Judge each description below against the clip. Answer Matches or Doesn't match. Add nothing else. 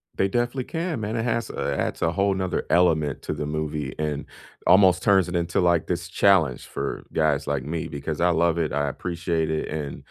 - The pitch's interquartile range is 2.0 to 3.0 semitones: Doesn't match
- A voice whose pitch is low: Matches